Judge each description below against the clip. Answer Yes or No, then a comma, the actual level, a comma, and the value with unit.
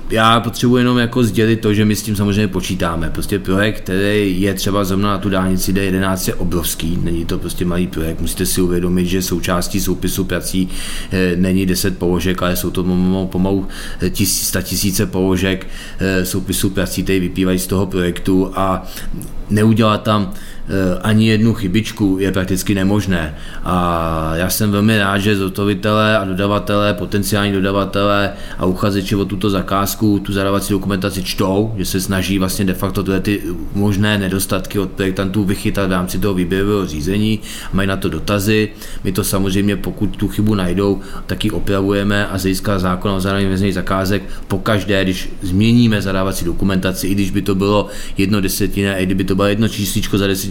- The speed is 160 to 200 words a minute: Yes, fast, 170 wpm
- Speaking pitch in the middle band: No, very low, 95 Hz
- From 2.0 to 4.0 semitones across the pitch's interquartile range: No, narrow, 1.6 semitones